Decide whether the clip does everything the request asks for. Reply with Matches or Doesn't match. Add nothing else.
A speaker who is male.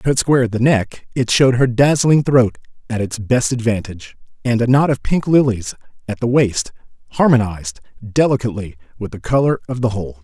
Matches